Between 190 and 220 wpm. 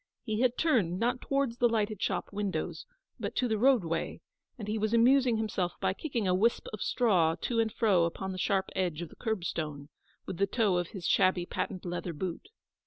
Yes: average, 200 wpm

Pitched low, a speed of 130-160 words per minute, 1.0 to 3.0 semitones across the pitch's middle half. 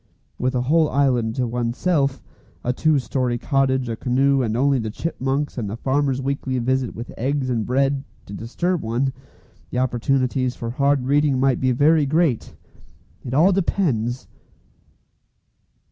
Yes: low, 130 Hz; average, 150 wpm; narrow, 2.5 semitones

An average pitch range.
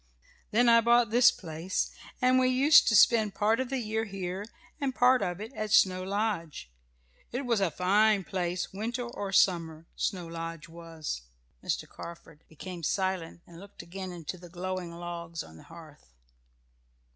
Yes: average, 4.7 semitones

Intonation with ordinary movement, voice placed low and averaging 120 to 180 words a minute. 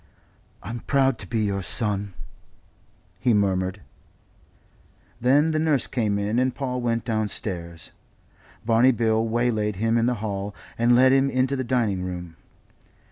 Yes: average, 3.8 semitones; low, 115 Hz; average, 140 wpm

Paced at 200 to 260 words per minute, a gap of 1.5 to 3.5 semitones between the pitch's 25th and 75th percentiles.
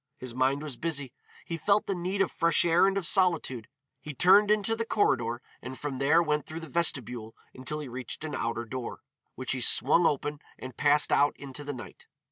No: fast, 205 wpm; average, 4.8 semitones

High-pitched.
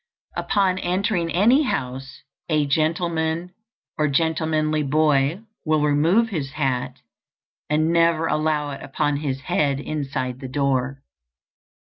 No: medium, 155 Hz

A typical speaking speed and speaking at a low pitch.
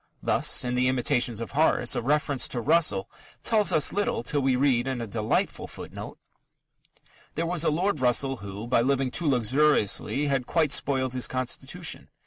Yes: average, 170 wpm; low, 130 Hz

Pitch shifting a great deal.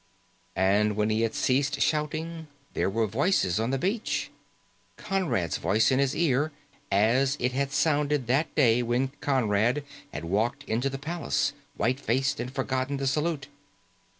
No: average, 4.3 semitones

